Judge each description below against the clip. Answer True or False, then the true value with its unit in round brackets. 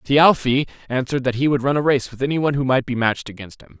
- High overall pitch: False (130 Hz)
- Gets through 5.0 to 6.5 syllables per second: False (6.8 syllables/s)